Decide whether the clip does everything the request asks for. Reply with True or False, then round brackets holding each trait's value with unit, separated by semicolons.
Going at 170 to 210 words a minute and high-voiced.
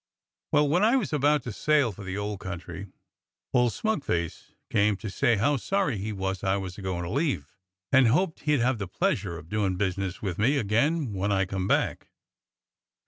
False (195 wpm; 105 Hz)